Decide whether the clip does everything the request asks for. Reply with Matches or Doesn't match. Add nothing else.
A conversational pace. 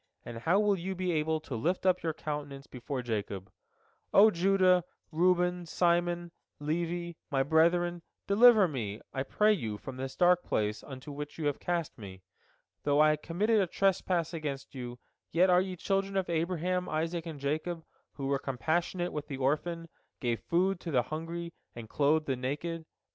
Matches